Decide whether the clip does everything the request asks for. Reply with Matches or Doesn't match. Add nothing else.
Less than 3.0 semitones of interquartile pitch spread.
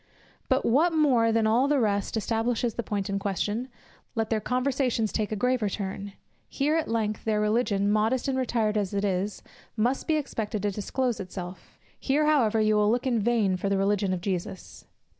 Doesn't match